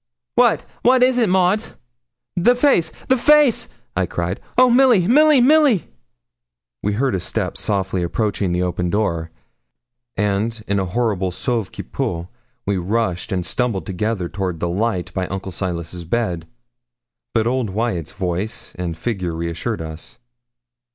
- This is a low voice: Yes, low, 100 Hz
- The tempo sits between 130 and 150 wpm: Yes, average, 145 wpm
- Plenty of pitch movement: Yes, wide, 7.4 semitones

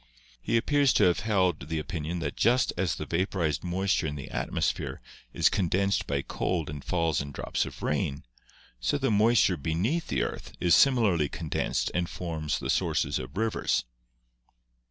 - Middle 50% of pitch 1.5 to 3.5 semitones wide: No, average, 4.9 semitones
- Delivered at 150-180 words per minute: Yes, average, 170 wpm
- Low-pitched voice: Yes, very low, 85 Hz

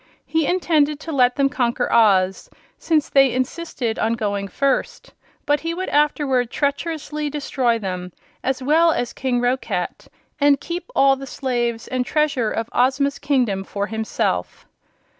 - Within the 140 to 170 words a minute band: Yes, average, 145 wpm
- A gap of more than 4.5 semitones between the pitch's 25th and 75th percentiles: No, average, 3.9 semitones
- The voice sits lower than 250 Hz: No, very high, 265 Hz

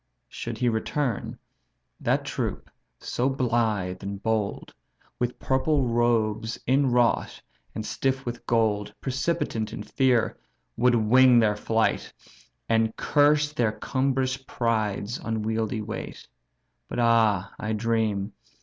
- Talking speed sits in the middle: No, slow, 115 wpm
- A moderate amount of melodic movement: Yes, average, 3.0 semitones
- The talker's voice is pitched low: Yes, low, 115 Hz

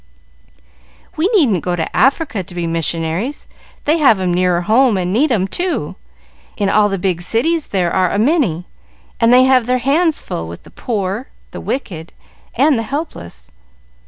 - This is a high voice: Yes, high, 210 Hz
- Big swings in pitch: Yes, wide, 7.3 semitones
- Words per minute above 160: Yes, average, 170 wpm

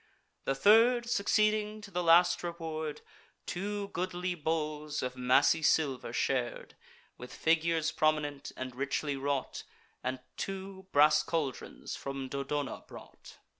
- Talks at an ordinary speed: No, slow, 120 wpm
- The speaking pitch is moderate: Yes, medium, 155 Hz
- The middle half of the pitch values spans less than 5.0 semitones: Yes, average, 4.6 semitones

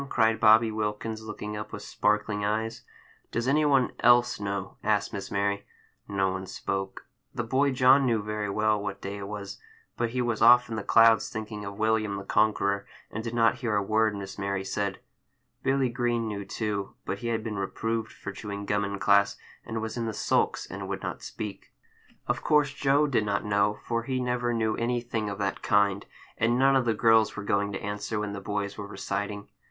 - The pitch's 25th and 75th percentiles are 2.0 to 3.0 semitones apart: Yes, narrow, 2.4 semitones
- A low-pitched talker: Yes, low, 105 Hz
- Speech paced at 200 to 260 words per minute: Yes, fast, 205 wpm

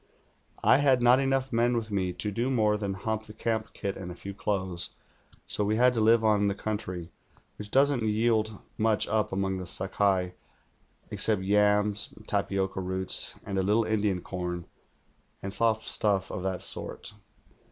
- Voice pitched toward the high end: No, low, 105 Hz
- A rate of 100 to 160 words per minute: No, average, 175 wpm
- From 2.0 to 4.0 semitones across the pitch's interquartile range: Yes, narrow, 2.5 semitones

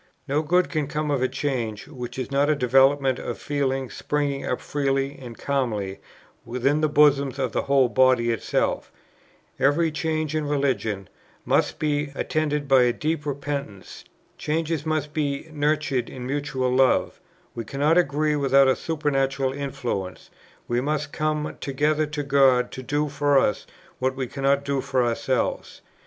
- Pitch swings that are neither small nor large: No, narrow, 2.3 semitones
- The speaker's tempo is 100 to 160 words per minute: Yes, average, 155 wpm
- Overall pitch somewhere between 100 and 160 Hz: Yes, medium, 140 Hz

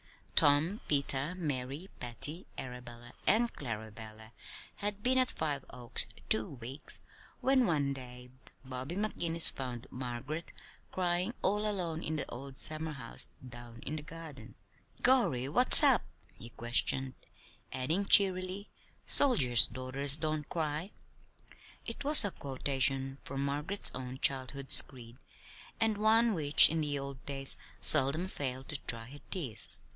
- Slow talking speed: Yes, slow, 130 wpm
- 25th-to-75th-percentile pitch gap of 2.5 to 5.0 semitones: No, wide, 5.4 semitones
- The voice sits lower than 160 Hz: Yes, medium, 140 Hz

